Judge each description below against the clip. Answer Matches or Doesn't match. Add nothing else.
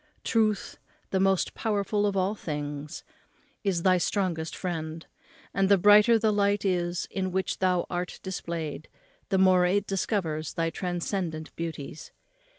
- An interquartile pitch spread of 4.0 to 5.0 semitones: Doesn't match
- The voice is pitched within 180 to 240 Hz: Matches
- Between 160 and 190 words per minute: Doesn't match